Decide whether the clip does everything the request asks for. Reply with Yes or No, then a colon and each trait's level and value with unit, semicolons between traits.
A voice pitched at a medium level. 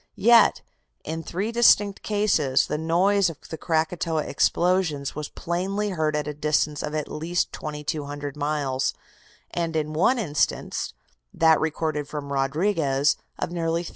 Yes: medium, 160 Hz